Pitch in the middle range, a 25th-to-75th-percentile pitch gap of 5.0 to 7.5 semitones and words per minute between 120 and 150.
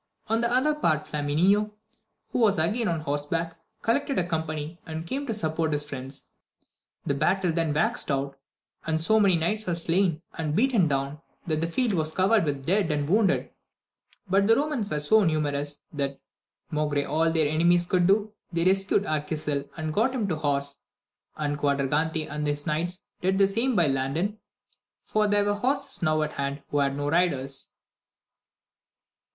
No: medium, 165 Hz; wide, 5.4 semitones; average, 175 wpm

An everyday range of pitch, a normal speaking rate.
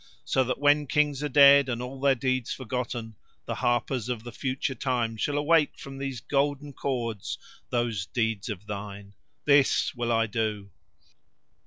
Yes: average, 3.5 semitones; average, 160 wpm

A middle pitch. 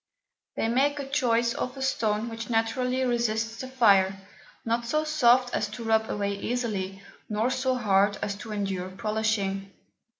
No: high, 225 Hz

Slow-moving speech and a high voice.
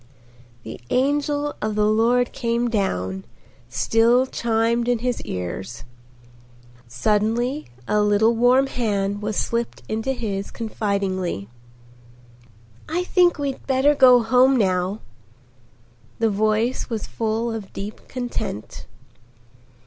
Yes: slow, 110 wpm; high, 225 Hz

